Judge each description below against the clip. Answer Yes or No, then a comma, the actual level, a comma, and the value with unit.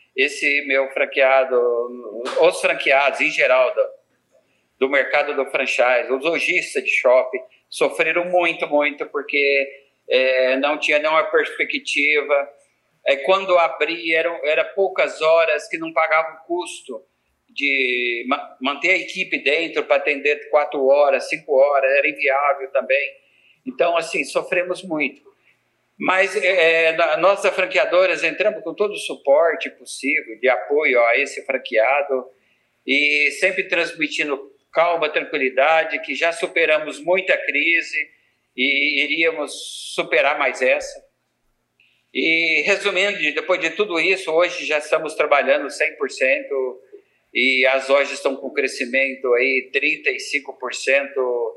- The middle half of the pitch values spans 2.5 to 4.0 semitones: No, average, 5.0 semitones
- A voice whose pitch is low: No, medium, 160 Hz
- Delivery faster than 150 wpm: No, average, 125 wpm